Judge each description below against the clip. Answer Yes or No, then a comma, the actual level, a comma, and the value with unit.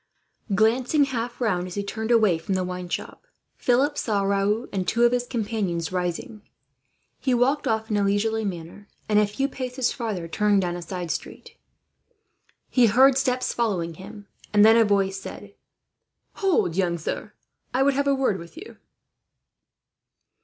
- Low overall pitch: No, high, 215 Hz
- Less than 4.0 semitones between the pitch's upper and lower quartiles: No, average, 4.6 semitones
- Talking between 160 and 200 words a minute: Yes, average, 165 wpm